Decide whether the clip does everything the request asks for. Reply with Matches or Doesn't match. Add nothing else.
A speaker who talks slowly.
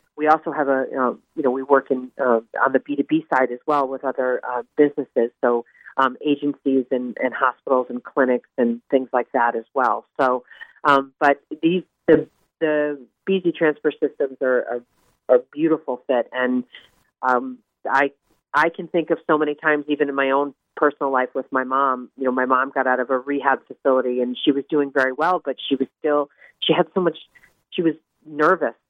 Doesn't match